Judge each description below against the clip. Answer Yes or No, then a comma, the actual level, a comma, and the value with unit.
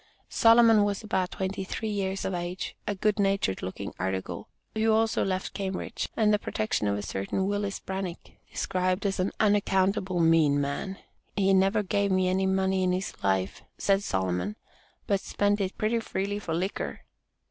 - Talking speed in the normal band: Yes, average, 170 wpm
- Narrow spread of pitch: Yes, narrow, 2.3 semitones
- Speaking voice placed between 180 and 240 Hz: Yes, high, 190 Hz